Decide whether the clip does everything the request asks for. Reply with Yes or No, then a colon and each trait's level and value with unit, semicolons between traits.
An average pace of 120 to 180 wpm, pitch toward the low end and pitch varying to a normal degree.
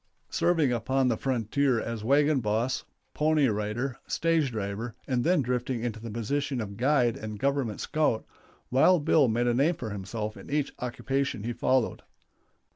Yes: average, 160 wpm; low, 125 Hz; average, 3.9 semitones